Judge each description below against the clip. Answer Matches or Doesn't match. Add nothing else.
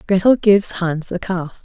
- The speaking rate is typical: Matches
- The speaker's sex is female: Matches